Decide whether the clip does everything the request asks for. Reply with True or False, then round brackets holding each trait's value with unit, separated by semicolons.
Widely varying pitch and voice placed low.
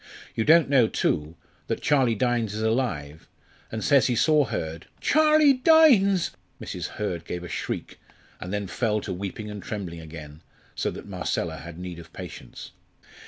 True (8.1 semitones; 105 Hz)